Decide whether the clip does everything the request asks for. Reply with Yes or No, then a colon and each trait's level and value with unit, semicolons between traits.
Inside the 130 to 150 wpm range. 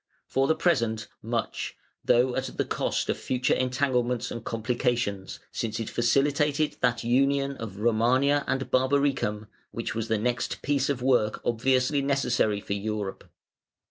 Yes: average, 140 wpm